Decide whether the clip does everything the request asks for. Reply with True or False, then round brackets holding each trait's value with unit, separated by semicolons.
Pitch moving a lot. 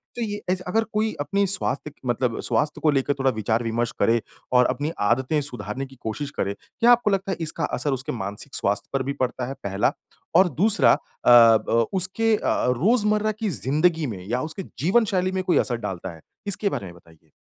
True (8.5 semitones)